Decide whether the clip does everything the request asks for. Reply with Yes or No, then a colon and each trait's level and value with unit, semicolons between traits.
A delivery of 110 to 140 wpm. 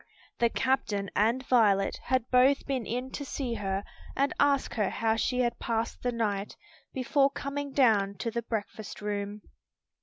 No: average, 155 wpm